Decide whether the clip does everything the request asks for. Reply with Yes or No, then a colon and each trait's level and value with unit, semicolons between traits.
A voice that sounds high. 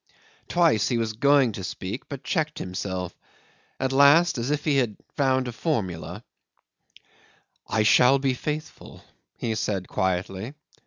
No: low, 125 Hz